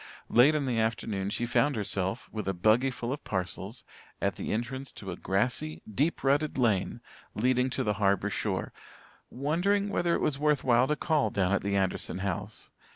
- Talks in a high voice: No, low, 120 Hz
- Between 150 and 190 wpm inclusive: Yes, average, 185 wpm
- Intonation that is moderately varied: No, wide, 5.7 semitones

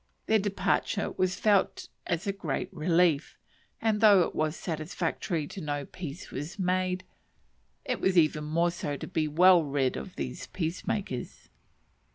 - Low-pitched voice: No, medium, 170 Hz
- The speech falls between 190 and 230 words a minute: No, average, 150 wpm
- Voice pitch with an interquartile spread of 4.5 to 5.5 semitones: No, average, 3.7 semitones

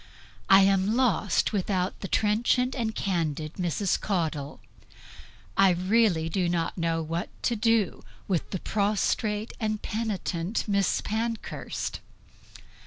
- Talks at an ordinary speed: No, slow, 115 wpm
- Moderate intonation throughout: Yes, average, 3.9 semitones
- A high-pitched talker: Yes, high, 195 Hz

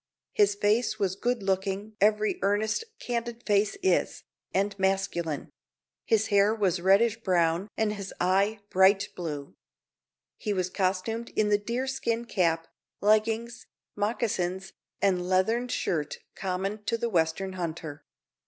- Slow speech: Yes, slow, 125 wpm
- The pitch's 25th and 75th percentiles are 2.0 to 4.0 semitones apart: Yes, average, 2.9 semitones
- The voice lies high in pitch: Yes, high, 200 Hz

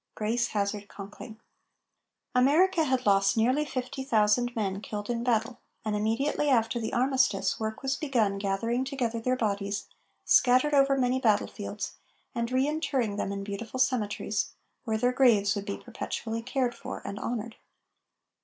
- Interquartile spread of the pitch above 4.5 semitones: No, average, 3.7 semitones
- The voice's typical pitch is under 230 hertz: No, high, 235 Hz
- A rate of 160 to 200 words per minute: No, average, 150 wpm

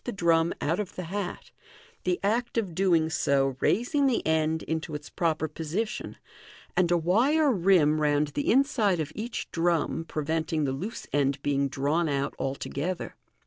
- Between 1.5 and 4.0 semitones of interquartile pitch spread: No, average, 4.6 semitones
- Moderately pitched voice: Yes, medium, 165 Hz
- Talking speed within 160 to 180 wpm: Yes, average, 170 wpm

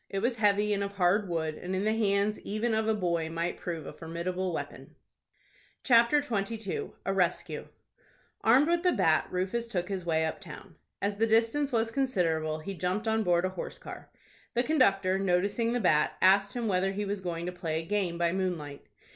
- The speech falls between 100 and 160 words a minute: No, average, 195 wpm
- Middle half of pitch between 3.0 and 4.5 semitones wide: Yes, average, 4.1 semitones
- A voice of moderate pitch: No, high, 195 Hz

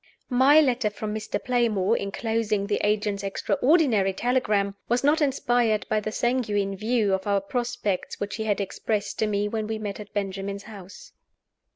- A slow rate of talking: No, average, 165 wpm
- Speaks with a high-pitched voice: Yes, high, 215 Hz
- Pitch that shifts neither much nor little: Yes, average, 3.2 semitones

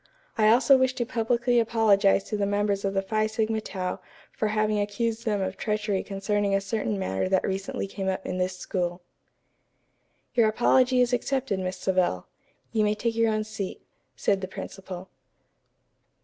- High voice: Yes, high, 210 Hz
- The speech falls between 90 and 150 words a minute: No, average, 170 wpm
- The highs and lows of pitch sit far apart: No, average, 2.7 semitones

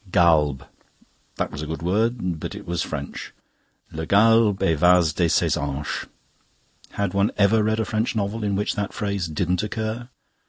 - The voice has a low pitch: Yes, low, 100 Hz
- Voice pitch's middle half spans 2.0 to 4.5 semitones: No, average, 5.0 semitones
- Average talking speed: Yes, average, 165 wpm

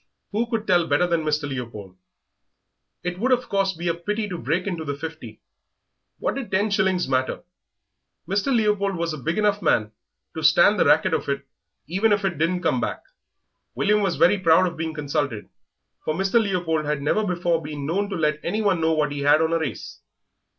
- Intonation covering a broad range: No, average, 4.6 semitones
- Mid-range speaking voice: Yes, medium, 170 Hz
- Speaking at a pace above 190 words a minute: Yes, average, 200 wpm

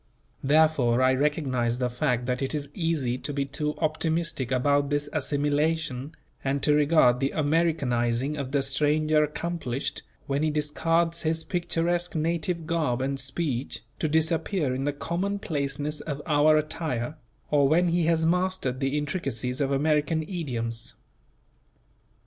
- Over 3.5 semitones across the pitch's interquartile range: No, average, 3.2 semitones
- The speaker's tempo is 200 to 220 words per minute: No, average, 140 wpm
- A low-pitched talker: No, medium, 150 Hz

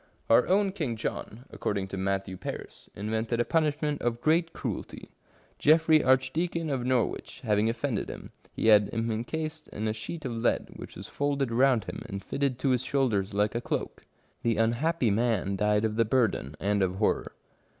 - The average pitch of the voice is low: Yes, low, 120 Hz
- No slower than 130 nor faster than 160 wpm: No, average, 180 wpm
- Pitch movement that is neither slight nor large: Yes, average, 5.0 semitones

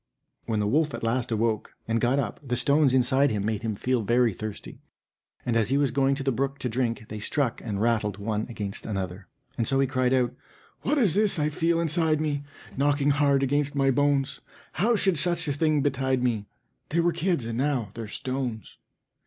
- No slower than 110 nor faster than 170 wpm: No, fast, 205 wpm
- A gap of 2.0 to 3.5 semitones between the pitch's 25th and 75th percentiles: No, average, 4.1 semitones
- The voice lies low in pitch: Yes, low, 130 Hz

